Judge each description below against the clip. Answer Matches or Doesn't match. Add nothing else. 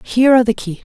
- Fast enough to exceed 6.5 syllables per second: Matches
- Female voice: Matches